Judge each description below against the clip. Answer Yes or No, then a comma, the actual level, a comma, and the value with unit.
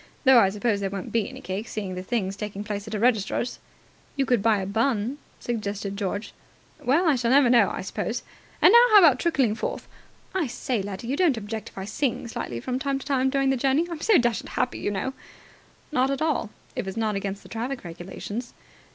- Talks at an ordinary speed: No, fast, 220 wpm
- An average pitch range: Yes, average, 4.9 semitones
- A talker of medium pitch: No, high, 230 Hz